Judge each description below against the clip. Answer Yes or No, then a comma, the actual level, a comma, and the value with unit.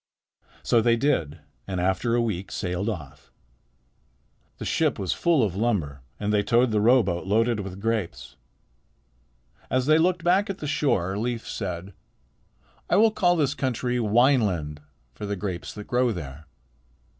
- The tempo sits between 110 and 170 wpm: Yes, average, 155 wpm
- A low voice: Yes, low, 110 Hz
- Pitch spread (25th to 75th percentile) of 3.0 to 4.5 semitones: No, average, 5.3 semitones